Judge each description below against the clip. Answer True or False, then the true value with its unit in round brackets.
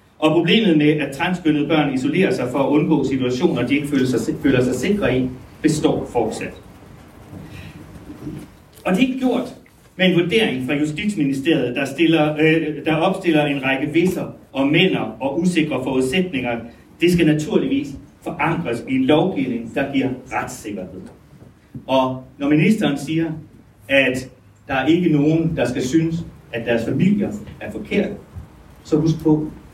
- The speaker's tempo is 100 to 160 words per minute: True (150 wpm)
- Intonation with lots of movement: False (4.0 semitones)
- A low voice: False (150 Hz)